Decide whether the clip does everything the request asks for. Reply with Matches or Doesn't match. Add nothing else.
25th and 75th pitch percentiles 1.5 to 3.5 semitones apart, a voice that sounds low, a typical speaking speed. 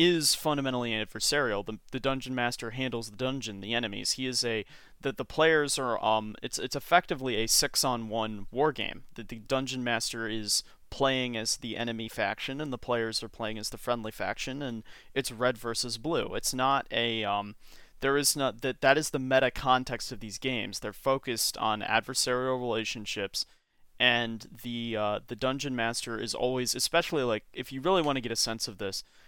Matches